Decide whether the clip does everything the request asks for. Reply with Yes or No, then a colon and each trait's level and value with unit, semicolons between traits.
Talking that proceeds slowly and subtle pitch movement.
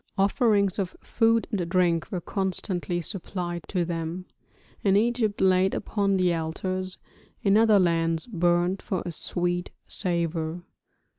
Yes: slow, 130 wpm; narrow, 2.3 semitones